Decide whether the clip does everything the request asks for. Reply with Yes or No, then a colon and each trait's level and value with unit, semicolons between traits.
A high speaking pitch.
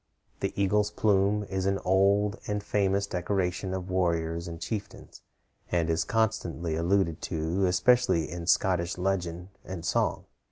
No: very low, 95 Hz